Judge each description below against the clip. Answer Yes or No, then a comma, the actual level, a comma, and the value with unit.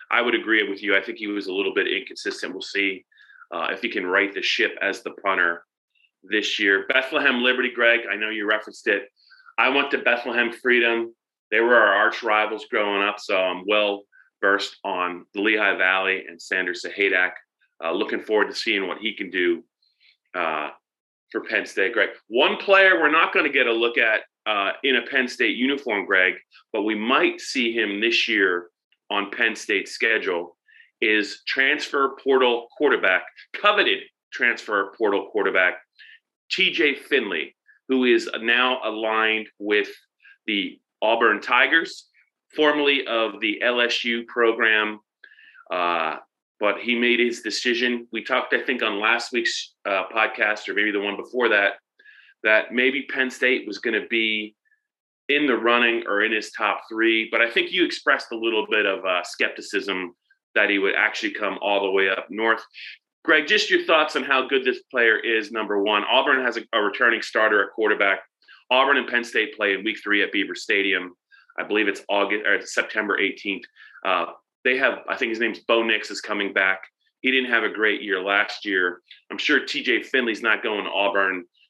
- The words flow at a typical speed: Yes, average, 180 wpm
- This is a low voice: Yes, low, 120 Hz